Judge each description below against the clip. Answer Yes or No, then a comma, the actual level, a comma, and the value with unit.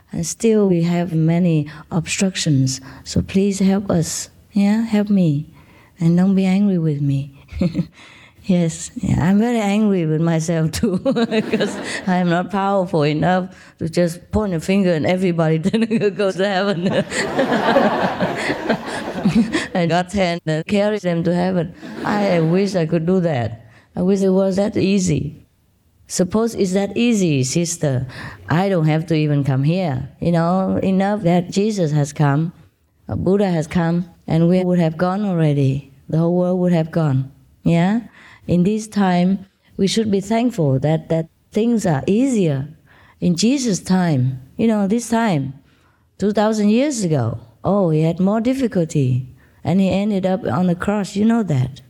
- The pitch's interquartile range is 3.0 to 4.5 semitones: Yes, average, 4.2 semitones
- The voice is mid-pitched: Yes, medium, 180 Hz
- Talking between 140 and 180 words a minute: Yes, average, 155 wpm